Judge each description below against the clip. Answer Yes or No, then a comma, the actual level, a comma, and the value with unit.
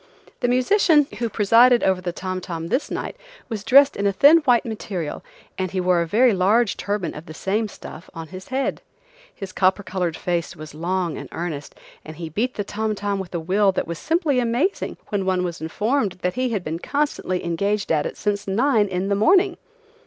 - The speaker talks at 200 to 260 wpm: Yes, fast, 205 wpm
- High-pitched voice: Yes, high, 200 Hz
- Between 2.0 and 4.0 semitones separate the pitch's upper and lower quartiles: No, average, 5.1 semitones